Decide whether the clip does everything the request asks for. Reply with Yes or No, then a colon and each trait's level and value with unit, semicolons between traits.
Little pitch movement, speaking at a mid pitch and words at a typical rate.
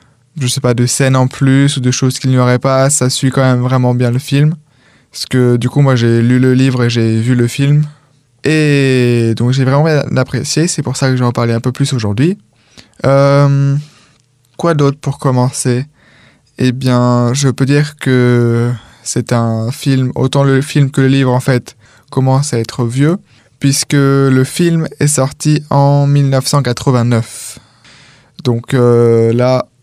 No: narrow, 2.3 semitones; low, 130 Hz; average, 180 wpm